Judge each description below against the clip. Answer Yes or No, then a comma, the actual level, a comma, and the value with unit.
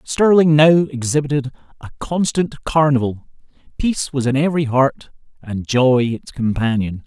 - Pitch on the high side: No, low, 135 Hz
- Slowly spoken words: Yes, slow, 125 wpm